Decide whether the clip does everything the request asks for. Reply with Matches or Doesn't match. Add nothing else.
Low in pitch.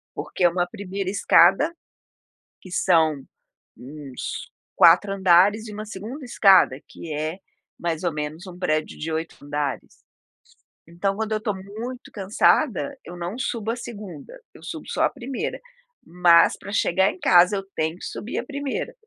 Doesn't match